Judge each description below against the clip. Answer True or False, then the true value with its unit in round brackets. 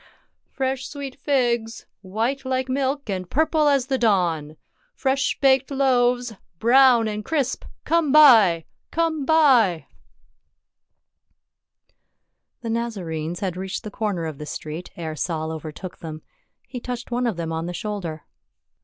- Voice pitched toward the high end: True (230 Hz)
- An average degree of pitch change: False (7.4 semitones)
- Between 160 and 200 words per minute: False (140 wpm)